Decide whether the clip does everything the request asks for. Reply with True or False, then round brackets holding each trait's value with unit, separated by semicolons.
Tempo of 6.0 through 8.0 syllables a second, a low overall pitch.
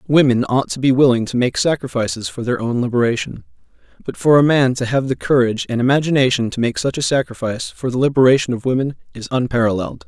True (6.5 syllables/s; 130 Hz)